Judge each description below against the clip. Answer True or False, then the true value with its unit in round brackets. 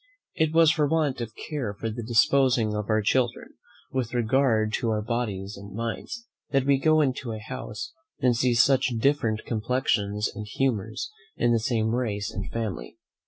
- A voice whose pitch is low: True (115 Hz)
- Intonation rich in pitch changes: False (3.5 semitones)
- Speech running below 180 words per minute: True (170 wpm)